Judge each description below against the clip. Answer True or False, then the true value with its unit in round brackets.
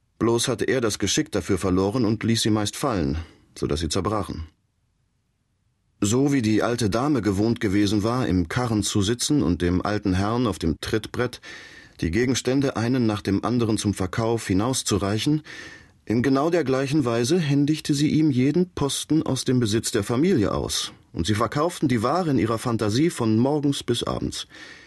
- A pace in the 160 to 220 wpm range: True (170 wpm)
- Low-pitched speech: True (115 Hz)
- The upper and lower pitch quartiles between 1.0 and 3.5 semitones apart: False (4.2 semitones)